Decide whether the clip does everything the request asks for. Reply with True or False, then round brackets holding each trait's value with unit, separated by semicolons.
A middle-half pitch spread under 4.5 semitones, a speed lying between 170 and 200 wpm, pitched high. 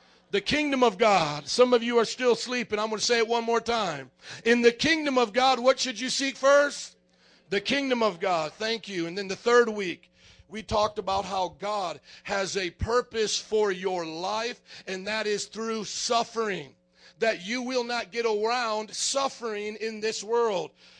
True (3.1 semitones; 185 wpm; 225 Hz)